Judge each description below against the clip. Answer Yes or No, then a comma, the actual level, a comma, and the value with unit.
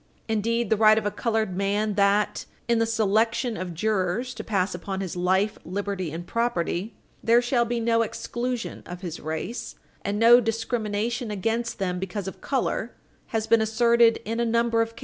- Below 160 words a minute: No, average, 180 wpm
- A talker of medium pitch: No, high, 220 Hz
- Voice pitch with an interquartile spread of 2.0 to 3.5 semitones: Yes, average, 2.9 semitones